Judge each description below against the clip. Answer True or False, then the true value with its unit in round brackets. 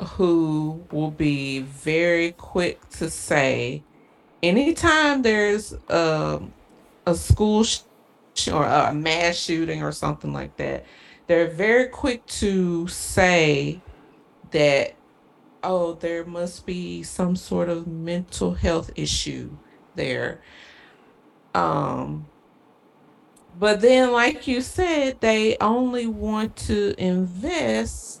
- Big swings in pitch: True (5.8 semitones)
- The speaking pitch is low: False (175 Hz)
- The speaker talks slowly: True (105 wpm)